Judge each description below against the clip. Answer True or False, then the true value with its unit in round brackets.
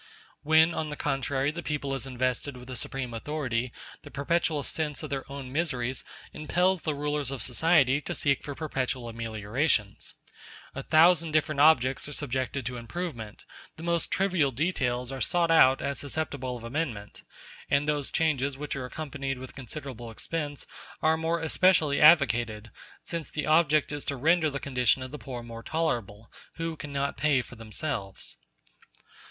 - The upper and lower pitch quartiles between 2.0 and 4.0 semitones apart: True (3.7 semitones)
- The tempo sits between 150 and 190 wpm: True (160 wpm)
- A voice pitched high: False (140 Hz)